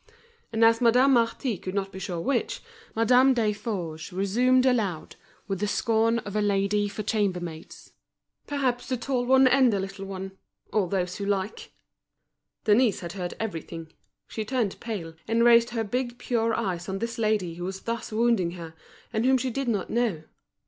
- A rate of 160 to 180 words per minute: Yes, average, 175 wpm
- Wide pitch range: No, average, 3.8 semitones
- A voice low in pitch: No, high, 215 Hz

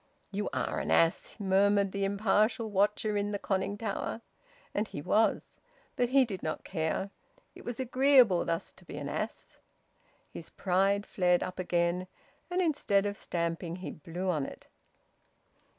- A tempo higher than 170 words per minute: No, average, 155 wpm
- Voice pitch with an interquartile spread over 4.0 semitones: No, average, 3.2 semitones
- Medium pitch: No, high, 200 Hz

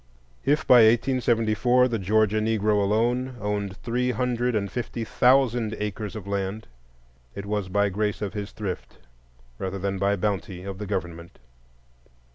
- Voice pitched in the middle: No, low, 105 Hz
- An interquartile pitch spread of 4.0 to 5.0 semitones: No, average, 3.1 semitones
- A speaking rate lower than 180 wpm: Yes, average, 145 wpm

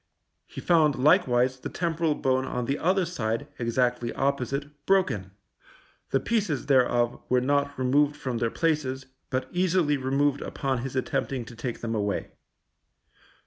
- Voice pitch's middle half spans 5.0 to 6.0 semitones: No, average, 3.1 semitones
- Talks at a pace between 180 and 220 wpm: No, average, 145 wpm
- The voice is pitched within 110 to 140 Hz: Yes, low, 135 Hz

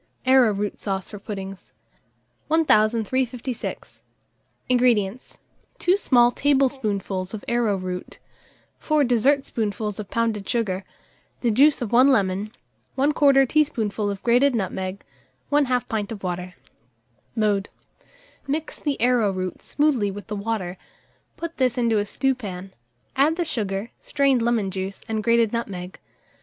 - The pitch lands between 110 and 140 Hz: No, high, 225 Hz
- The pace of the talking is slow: Yes, slow, 120 wpm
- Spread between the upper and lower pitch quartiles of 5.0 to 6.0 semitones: No, average, 4.6 semitones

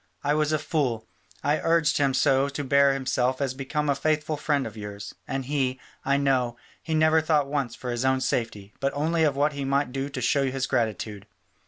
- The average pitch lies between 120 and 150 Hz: Yes, medium, 140 Hz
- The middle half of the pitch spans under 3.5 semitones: Yes, narrow, 2.5 semitones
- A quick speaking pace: Yes, fast, 210 wpm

